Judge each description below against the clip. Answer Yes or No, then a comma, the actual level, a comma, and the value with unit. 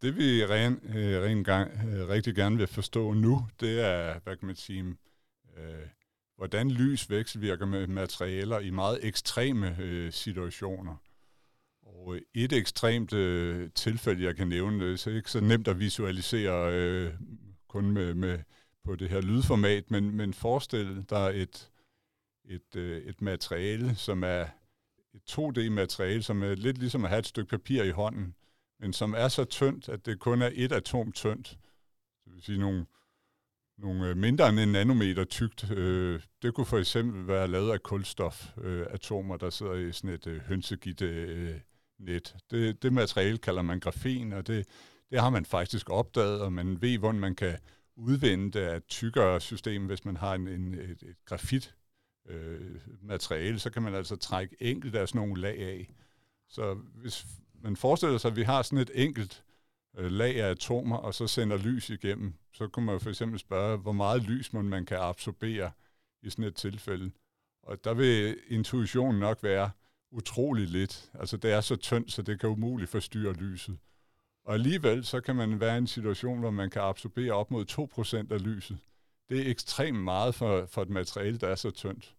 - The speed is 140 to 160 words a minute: No, average, 175 wpm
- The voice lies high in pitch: No, low, 105 Hz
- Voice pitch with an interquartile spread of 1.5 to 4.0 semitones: Yes, average, 3.6 semitones